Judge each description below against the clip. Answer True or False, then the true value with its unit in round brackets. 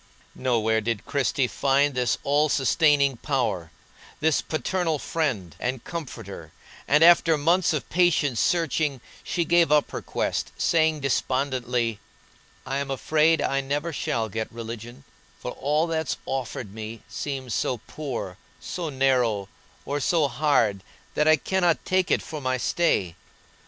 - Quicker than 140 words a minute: False (135 wpm)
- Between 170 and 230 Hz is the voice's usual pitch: False (140 Hz)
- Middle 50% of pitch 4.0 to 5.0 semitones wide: True (4.5 semitones)